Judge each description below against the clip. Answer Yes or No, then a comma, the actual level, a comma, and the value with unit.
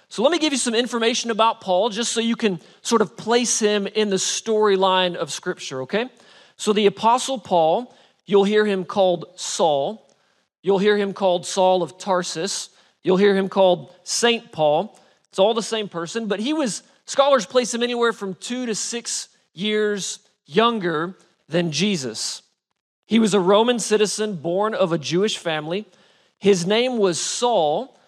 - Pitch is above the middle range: Yes, high, 205 Hz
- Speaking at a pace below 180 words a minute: Yes, average, 170 wpm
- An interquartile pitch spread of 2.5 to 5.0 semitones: Yes, average, 4.0 semitones